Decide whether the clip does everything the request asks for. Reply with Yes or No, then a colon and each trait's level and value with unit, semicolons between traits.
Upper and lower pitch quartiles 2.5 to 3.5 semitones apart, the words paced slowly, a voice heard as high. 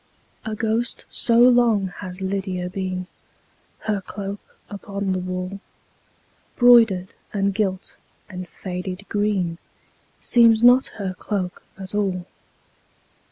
Yes: average, 2.9 semitones; slow, 110 wpm; high, 195 Hz